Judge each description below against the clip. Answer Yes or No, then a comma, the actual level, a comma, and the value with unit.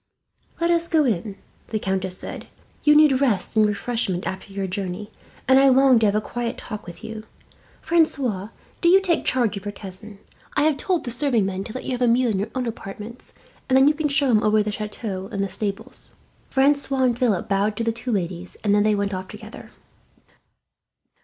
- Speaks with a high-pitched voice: Yes, high, 220 Hz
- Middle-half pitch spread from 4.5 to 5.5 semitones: Yes, average, 4.8 semitones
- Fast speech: Yes, fast, 210 wpm